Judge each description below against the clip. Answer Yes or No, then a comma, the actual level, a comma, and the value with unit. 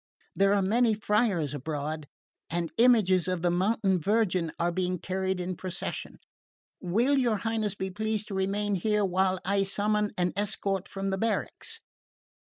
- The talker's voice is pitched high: Yes, high, 195 Hz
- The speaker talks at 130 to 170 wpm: Yes, average, 155 wpm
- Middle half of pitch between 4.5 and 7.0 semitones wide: No, narrow, 2.6 semitones